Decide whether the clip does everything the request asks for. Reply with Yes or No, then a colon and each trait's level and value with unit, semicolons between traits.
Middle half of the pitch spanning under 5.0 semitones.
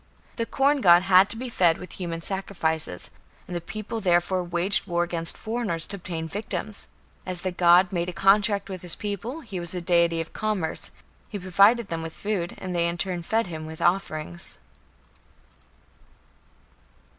Yes: average, 2.9 semitones